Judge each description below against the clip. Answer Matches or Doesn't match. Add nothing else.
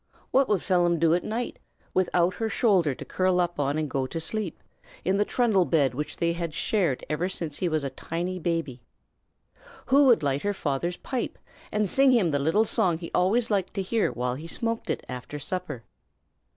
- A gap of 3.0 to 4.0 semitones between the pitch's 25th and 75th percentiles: Doesn't match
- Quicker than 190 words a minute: Matches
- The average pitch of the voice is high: Doesn't match